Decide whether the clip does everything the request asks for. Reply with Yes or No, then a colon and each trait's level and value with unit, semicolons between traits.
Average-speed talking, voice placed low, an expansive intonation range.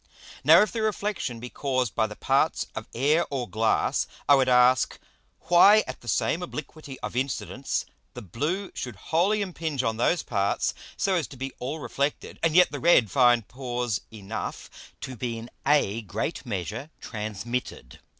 Yes: average, 170 wpm; low, 130 Hz; wide, 5.7 semitones